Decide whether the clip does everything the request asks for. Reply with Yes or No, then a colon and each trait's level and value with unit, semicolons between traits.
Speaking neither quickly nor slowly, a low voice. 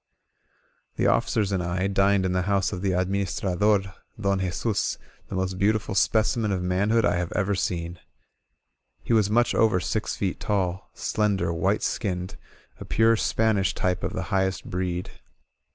Yes: average, 170 wpm; very low, 95 Hz